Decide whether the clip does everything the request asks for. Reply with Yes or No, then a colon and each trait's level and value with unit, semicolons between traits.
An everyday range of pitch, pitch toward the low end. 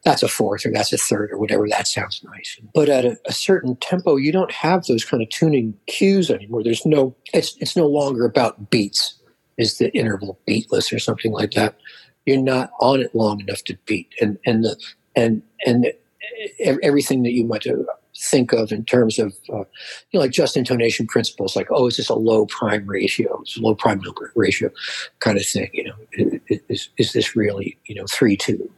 Yes: average, 4.1 semitones; low, 120 Hz